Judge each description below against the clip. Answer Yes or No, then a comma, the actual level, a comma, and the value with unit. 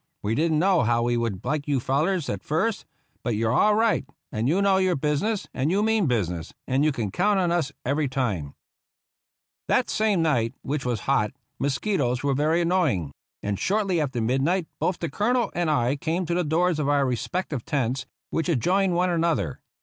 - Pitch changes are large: Yes, wide, 6.6 semitones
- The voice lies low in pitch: No, medium, 150 Hz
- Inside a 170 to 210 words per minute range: Yes, average, 195 wpm